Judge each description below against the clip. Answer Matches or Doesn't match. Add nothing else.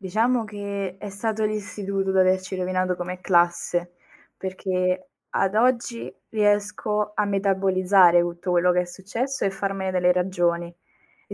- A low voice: Doesn't match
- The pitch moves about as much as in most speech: Doesn't match